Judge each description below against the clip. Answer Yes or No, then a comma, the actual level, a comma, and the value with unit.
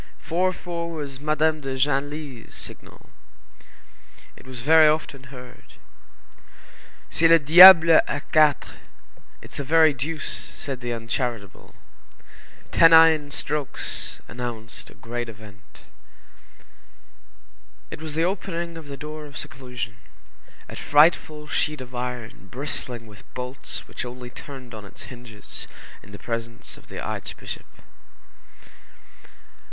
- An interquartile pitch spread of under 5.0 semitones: Yes, average, 4.3 semitones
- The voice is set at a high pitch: No, medium, 140 Hz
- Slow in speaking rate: Yes, slow, 115 wpm